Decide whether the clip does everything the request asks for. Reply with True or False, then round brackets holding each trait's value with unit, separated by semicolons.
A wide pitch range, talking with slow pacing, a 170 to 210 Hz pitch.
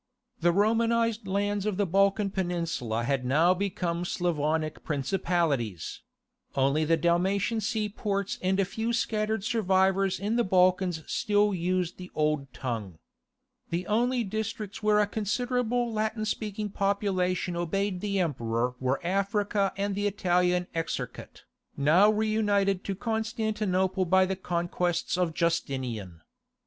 False (3.6 semitones; 125 wpm; 190 Hz)